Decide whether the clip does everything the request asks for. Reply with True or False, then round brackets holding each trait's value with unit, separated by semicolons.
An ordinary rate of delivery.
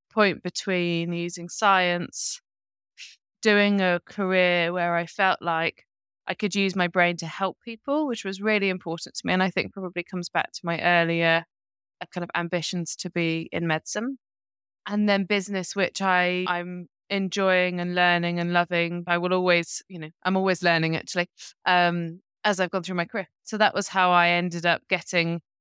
True (180 wpm)